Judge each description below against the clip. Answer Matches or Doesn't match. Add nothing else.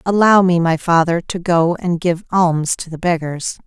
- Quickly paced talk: Doesn't match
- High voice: Doesn't match